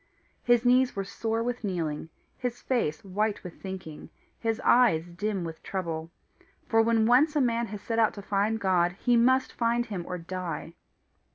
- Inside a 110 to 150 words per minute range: No, average, 175 wpm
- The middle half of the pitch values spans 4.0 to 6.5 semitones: Yes, average, 4.7 semitones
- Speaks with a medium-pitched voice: No, high, 215 Hz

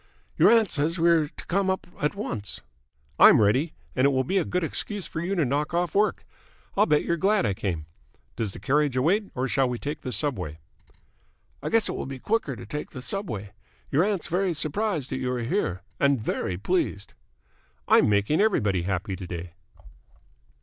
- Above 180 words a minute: Yes, average, 200 wpm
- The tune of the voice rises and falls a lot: Yes, wide, 8.5 semitones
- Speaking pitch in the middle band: Yes, medium, 145 Hz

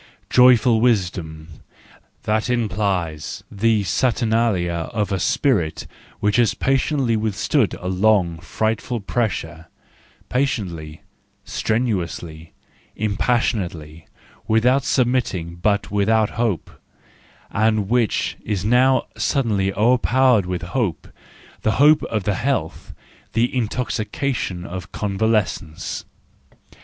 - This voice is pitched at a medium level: No, low, 105 Hz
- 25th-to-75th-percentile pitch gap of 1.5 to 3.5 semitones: No, average, 4.8 semitones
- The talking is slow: Yes, slow, 90 wpm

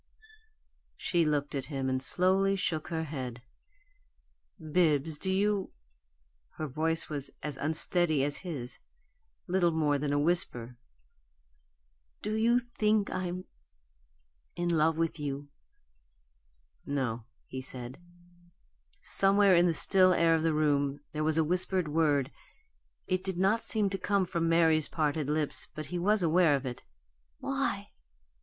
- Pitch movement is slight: No, average, 4.2 semitones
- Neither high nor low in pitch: Yes, medium, 160 Hz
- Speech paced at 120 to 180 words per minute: Yes, average, 140 wpm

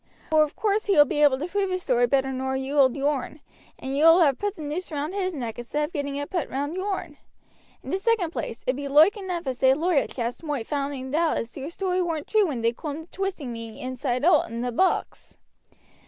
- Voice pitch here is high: Yes, very high, 295 Hz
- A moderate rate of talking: No, fast, 240 wpm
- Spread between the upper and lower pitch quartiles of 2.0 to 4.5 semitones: No, average, 5.1 semitones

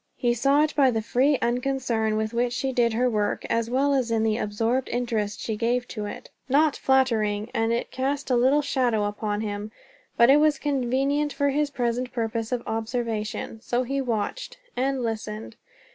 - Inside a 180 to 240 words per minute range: Yes, average, 185 wpm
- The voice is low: No, high, 240 Hz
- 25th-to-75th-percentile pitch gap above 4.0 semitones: No, average, 3.3 semitones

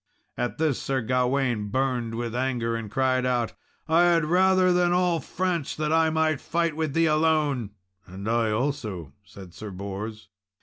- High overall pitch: No, low, 130 Hz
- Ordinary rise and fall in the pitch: No, wide, 5.9 semitones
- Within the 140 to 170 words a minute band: Yes, average, 165 wpm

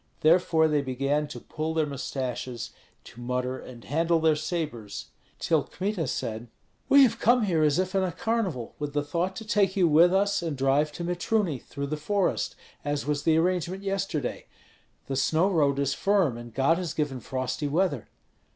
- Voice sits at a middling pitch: Yes, medium, 155 Hz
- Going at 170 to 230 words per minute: Yes, average, 180 wpm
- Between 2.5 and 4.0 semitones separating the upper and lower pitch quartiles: No, average, 4.9 semitones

